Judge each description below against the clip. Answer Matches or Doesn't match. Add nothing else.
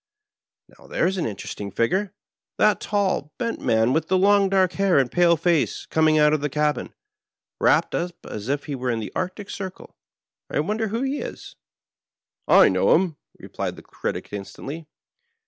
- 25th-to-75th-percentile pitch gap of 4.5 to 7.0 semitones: Matches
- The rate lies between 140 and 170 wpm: Doesn't match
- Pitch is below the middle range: Doesn't match